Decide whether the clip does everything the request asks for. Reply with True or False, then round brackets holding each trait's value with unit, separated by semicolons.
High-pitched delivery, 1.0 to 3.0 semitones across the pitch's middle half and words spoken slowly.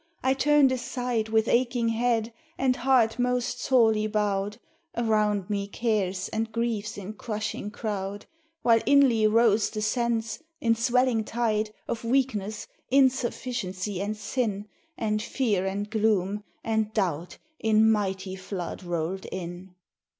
True (220 Hz; 2.7 semitones; 130 wpm)